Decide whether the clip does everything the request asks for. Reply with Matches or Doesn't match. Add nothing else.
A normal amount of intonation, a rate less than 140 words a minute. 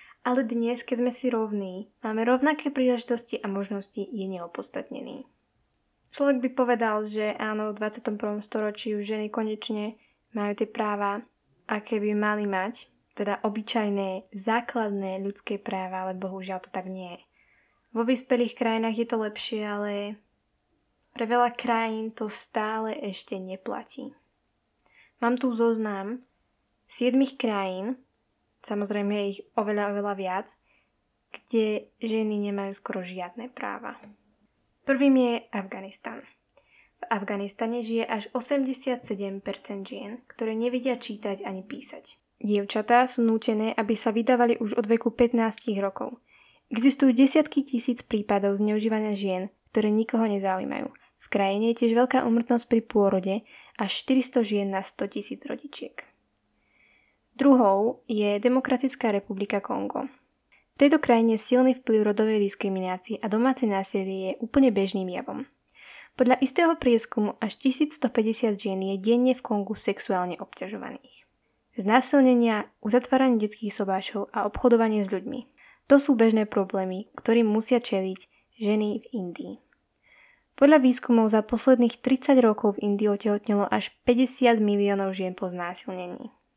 Matches